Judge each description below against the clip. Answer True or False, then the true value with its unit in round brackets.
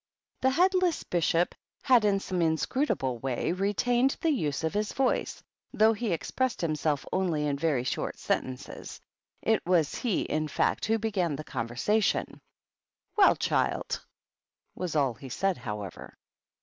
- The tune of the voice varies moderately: False (7.2 semitones)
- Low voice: False (180 Hz)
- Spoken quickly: False (145 wpm)